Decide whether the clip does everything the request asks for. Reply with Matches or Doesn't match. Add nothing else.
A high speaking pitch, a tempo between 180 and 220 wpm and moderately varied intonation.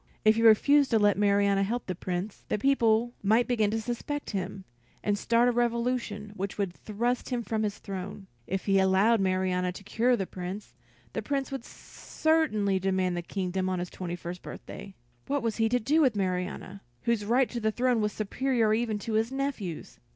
Matches